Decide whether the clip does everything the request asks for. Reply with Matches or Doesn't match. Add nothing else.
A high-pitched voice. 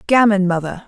Matches